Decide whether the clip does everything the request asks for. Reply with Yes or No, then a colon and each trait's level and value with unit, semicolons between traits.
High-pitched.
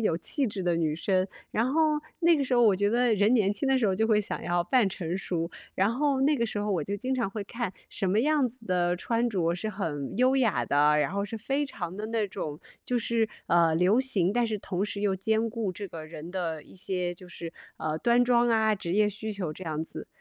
Yes: high, 205 Hz